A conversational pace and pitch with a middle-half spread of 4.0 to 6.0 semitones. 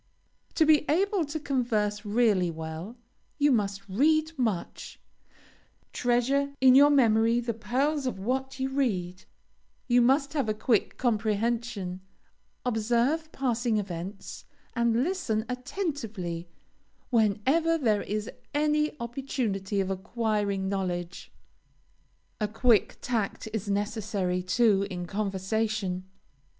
No: slow, 110 wpm; average, 4.9 semitones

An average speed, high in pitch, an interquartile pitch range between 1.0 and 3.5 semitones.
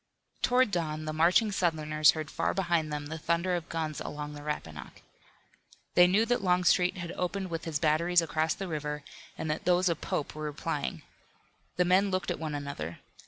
No: average, 185 wpm; medium, 165 Hz; average, 2.9 semitones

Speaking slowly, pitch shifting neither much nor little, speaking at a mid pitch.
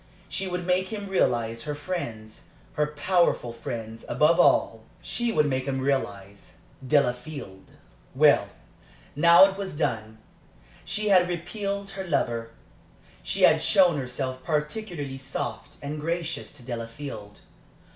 No: slow, 125 wpm; wide, 6.9 semitones; medium, 145 Hz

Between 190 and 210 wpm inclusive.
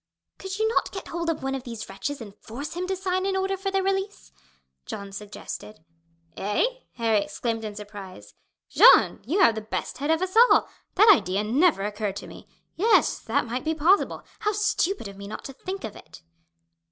Yes: average, 200 wpm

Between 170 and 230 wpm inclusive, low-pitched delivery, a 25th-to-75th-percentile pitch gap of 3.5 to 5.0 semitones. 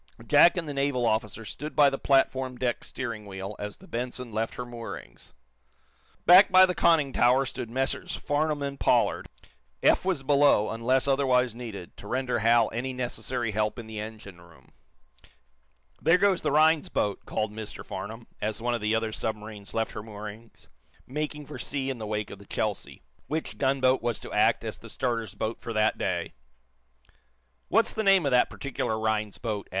Yes: average, 180 wpm; low, 120 Hz; average, 4.2 semitones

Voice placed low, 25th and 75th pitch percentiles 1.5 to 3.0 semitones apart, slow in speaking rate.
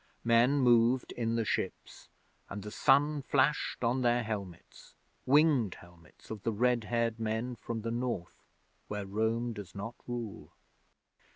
No: low, 115 Hz; narrow, 2.5 semitones; average, 145 wpm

